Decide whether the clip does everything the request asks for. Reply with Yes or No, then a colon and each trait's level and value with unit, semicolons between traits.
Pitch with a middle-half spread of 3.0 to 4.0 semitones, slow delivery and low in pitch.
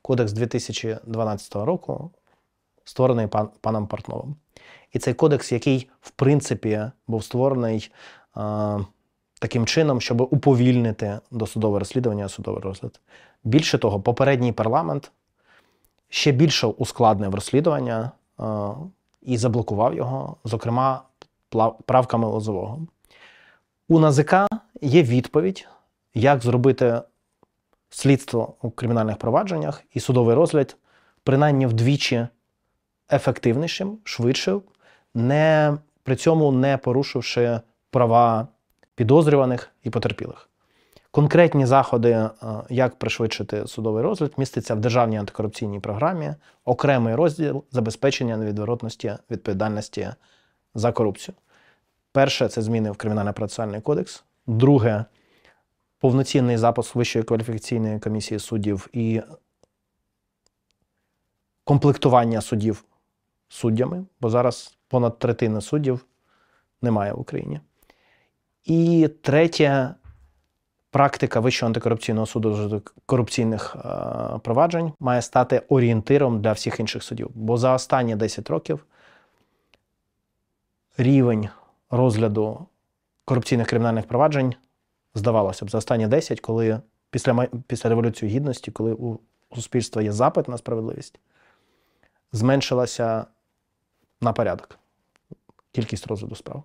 Yes: average, 3.4 semitones; slow, 95 wpm; low, 120 Hz